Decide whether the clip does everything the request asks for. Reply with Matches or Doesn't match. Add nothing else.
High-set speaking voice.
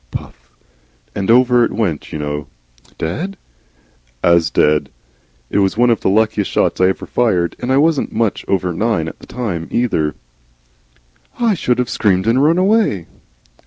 Doesn't match